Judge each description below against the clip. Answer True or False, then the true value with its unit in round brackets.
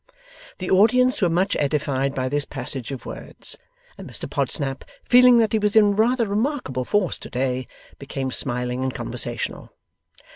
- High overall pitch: False (150 Hz)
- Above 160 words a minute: False (155 wpm)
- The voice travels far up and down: True (8.6 semitones)